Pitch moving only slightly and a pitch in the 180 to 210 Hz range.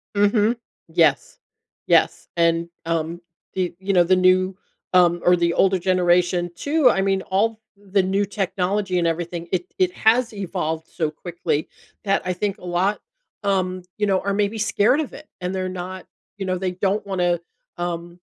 Yes: narrow, 2.3 semitones; medium, 185 Hz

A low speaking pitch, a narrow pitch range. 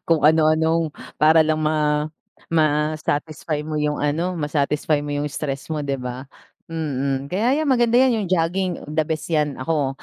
No: medium, 155 Hz; narrow, 1.9 semitones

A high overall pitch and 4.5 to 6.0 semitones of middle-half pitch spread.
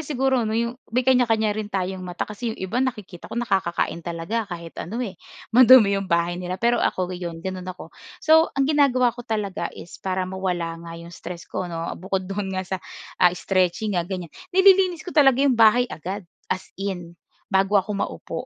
Yes: high, 195 Hz; average, 5.0 semitones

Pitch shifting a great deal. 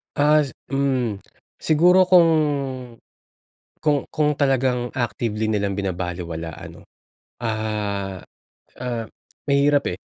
Yes: wide, 6.0 semitones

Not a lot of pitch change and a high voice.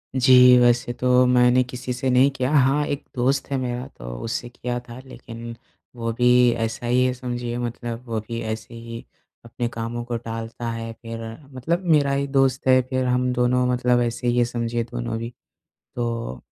No: narrow, 1.4 semitones; low, 120 Hz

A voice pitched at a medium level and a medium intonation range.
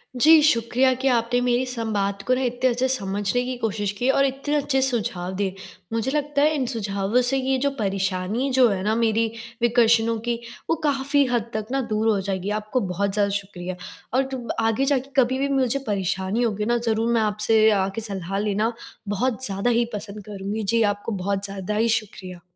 No: high, 225 Hz; average, 4.1 semitones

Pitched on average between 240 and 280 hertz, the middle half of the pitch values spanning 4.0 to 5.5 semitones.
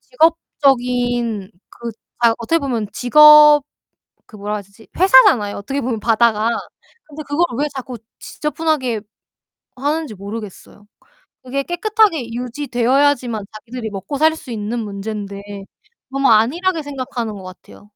Yes: high, 245 Hz; average, 5.2 semitones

